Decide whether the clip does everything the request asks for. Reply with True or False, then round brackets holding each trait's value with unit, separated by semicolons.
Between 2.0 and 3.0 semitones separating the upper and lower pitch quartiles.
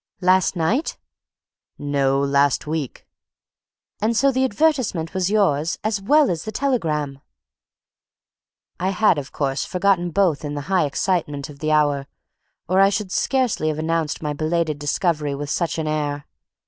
False (5.1 semitones)